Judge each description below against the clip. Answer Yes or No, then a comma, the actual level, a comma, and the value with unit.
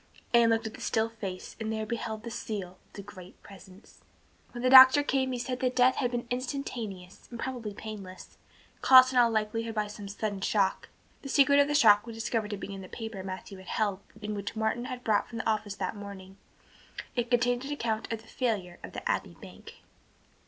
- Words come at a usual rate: No, fast, 215 wpm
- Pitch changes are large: No, average, 3.4 semitones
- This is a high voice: Yes, high, 220 Hz